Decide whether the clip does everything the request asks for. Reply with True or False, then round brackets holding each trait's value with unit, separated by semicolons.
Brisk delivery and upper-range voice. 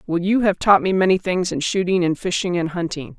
False (245 wpm; 180 Hz)